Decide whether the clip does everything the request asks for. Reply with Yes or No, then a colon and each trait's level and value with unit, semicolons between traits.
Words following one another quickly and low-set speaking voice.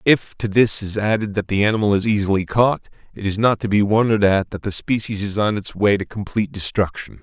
Yes: fast, 235 wpm; low, 105 Hz